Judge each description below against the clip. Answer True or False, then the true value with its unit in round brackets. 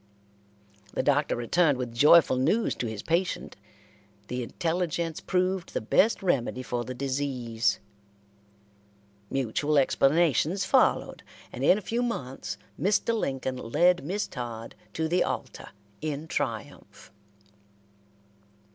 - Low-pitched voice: False (145 Hz)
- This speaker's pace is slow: True (115 wpm)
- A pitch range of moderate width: False (5.8 semitones)